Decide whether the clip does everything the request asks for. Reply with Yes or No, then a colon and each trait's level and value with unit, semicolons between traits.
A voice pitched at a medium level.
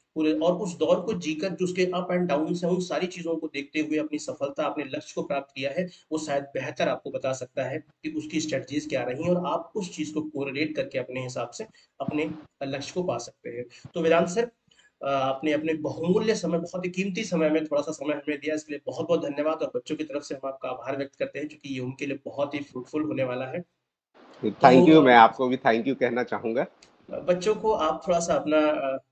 Yes: medium, 155 Hz